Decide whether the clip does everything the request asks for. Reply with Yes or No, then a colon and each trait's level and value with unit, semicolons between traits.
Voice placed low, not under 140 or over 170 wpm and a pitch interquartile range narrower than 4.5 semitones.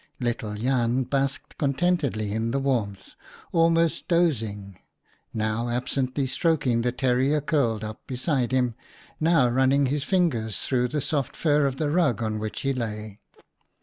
Yes: low, 130 Hz; average, 150 wpm; average, 4.1 semitones